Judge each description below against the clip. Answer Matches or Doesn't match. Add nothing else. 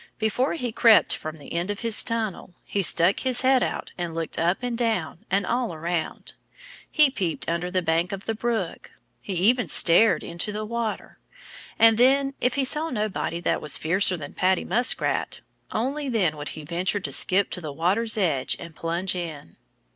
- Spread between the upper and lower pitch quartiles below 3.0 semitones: Doesn't match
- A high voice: Matches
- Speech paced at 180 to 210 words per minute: Matches